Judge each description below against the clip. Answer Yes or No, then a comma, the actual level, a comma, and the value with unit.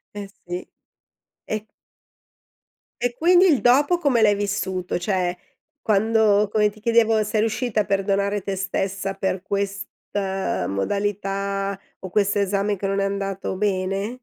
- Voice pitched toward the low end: No, high, 200 Hz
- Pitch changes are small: Yes, narrow, 1.7 semitones